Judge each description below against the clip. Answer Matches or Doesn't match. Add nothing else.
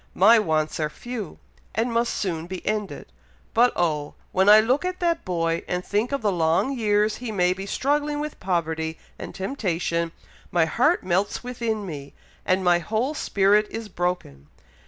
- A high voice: Matches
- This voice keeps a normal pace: Matches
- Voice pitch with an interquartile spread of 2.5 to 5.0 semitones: Doesn't match